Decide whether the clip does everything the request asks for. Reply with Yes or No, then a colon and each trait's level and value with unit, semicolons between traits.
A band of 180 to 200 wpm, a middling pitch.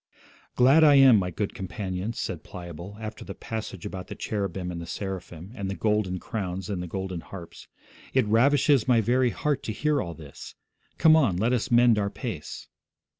No: average, 185 wpm; low, 105 Hz